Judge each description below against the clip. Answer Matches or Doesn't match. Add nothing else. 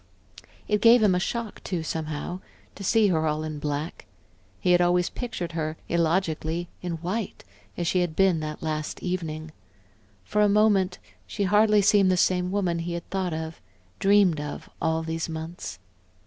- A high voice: Doesn't match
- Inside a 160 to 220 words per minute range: Matches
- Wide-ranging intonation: Doesn't match